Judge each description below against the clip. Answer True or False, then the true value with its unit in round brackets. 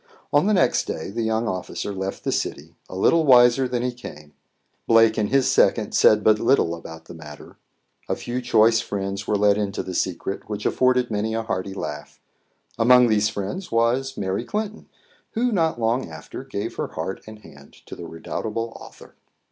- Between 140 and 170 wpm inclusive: False (185 wpm)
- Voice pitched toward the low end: True (110 Hz)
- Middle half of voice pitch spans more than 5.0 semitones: False (4.2 semitones)